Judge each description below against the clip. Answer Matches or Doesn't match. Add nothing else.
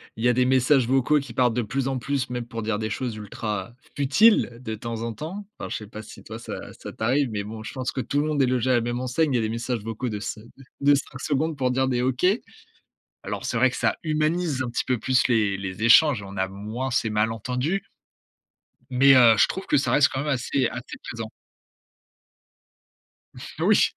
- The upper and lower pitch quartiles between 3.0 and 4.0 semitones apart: Matches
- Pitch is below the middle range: Matches